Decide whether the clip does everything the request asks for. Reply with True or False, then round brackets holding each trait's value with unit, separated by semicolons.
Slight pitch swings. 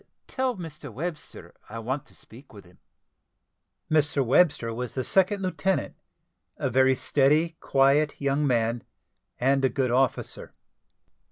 False (3.6 semitones)